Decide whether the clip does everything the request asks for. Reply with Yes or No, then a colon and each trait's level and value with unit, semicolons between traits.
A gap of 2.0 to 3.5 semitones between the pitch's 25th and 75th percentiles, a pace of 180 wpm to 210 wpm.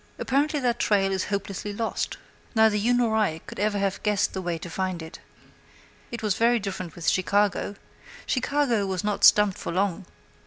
Yes: average, 2.9 semitones; average, 185 wpm